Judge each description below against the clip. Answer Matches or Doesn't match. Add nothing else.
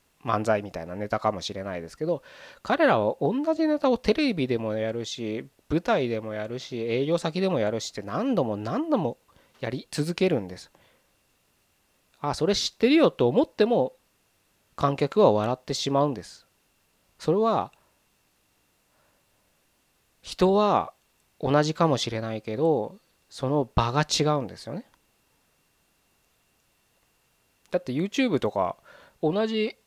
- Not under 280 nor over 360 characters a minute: Doesn't match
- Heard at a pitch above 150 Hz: Doesn't match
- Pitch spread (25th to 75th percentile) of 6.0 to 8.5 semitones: Matches